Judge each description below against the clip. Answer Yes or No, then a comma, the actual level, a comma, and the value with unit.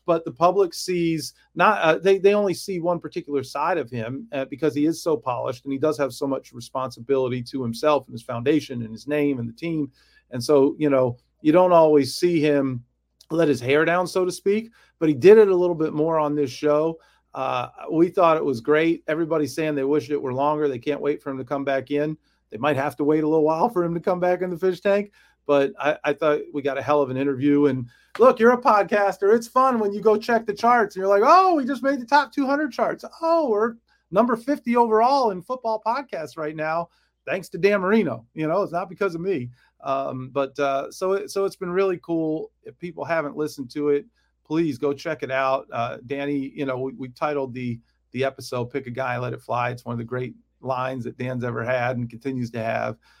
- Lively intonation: Yes, wide, 5.8 semitones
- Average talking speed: No, fast, 240 wpm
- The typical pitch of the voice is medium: Yes, medium, 155 Hz